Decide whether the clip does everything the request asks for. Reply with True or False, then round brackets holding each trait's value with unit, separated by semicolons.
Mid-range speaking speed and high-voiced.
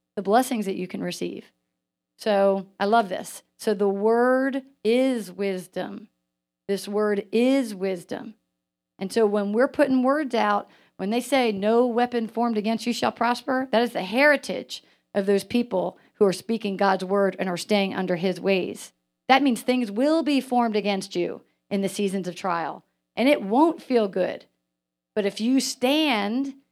True (170 wpm; 210 Hz)